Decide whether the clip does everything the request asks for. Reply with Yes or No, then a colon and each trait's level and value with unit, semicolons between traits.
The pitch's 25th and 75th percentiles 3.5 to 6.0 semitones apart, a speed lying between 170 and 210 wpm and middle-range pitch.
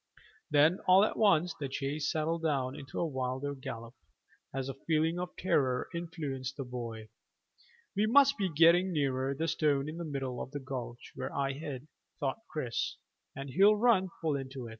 Yes: average, 4.2 semitones; average, 180 wpm; medium, 145 Hz